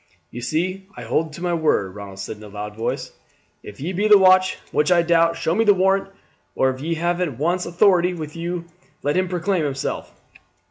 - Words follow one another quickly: Yes, fast, 215 wpm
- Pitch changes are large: No, average, 4.3 semitones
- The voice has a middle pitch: Yes, medium, 170 Hz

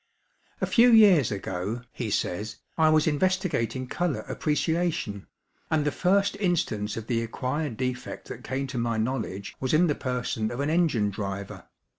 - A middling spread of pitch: No, wide, 6.5 semitones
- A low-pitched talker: Yes, low, 130 Hz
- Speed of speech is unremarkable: Yes, average, 160 wpm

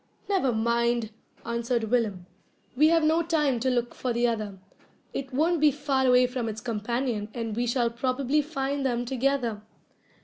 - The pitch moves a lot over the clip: No, average, 2.8 semitones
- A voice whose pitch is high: Yes, high, 245 Hz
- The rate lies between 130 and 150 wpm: No, average, 165 wpm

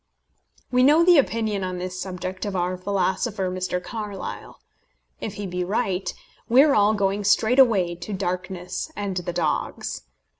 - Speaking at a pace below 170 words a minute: Yes, average, 155 wpm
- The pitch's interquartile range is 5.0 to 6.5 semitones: No, average, 3.1 semitones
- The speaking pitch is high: Yes, high, 195 Hz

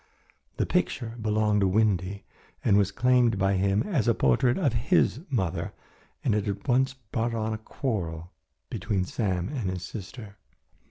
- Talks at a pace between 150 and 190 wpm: Yes, average, 160 wpm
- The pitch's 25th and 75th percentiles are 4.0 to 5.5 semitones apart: No, average, 3.6 semitones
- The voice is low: Yes, low, 105 Hz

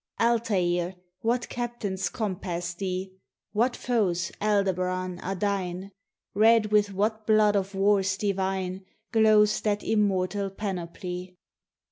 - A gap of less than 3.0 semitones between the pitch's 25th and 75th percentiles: Yes, narrow, 2.5 semitones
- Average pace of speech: No, slow, 105 wpm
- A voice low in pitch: No, high, 195 Hz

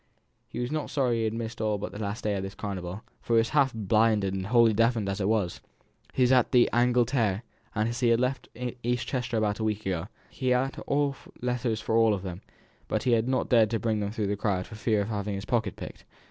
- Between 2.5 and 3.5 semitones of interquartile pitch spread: Yes, average, 2.9 semitones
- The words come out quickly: Yes, fast, 230 wpm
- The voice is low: Yes, low, 110 Hz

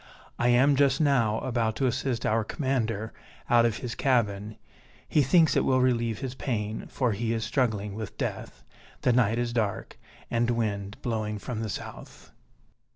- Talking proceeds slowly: No, average, 165 wpm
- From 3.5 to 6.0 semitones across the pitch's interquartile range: No, average, 2.8 semitones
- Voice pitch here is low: Yes, low, 115 Hz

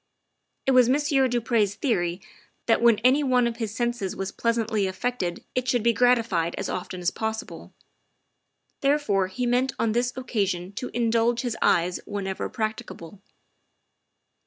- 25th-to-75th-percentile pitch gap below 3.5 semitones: No, average, 4.1 semitones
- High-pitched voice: Yes, high, 230 Hz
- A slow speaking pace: No, average, 155 wpm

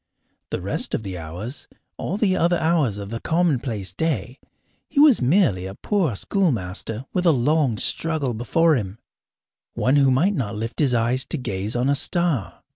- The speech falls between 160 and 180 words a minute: Yes, average, 175 wpm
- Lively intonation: Yes, wide, 7.1 semitones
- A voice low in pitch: Yes, low, 130 Hz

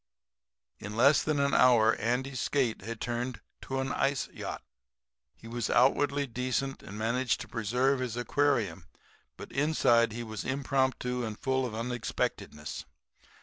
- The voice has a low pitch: Yes, low, 125 Hz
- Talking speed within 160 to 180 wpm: No, average, 145 wpm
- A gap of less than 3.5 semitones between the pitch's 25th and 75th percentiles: Yes, average, 2.8 semitones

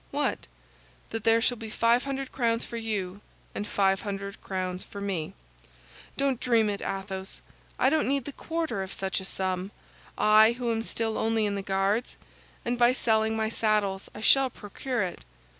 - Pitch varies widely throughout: No, average, 3.5 semitones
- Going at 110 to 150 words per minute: No, average, 170 wpm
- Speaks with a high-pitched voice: Yes, high, 220 Hz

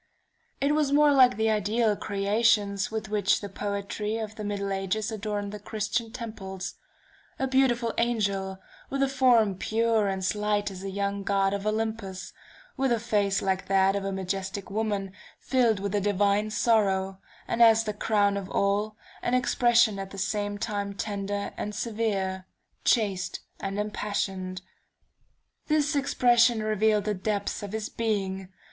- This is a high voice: Yes, high, 210 Hz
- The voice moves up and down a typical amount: No, narrow, 2.2 semitones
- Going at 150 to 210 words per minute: Yes, average, 155 wpm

